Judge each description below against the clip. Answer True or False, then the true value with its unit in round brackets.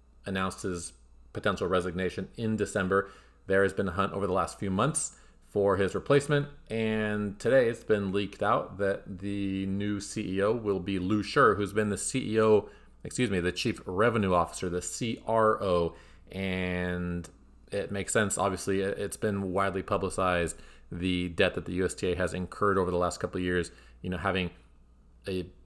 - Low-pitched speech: True (95 Hz)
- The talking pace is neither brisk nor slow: True (165 wpm)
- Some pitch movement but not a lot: False (2.3 semitones)